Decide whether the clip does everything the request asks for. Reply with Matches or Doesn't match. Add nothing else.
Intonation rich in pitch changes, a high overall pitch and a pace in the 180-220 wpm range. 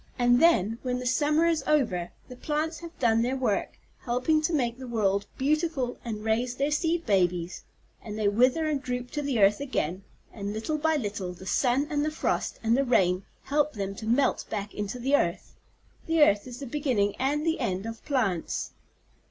Matches